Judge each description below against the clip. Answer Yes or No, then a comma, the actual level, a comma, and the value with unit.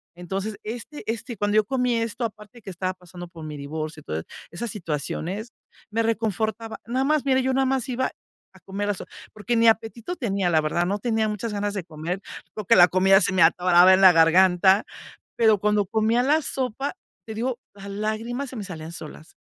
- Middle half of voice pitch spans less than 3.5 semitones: No, average, 4.2 semitones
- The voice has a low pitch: No, high, 205 Hz